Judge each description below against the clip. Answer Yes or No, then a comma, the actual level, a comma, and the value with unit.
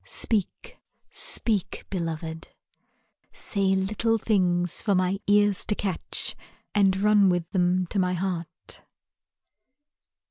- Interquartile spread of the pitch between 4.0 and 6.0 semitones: No, narrow, 2.5 semitones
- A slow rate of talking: Yes, slow, 105 wpm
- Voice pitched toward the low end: No, high, 190 Hz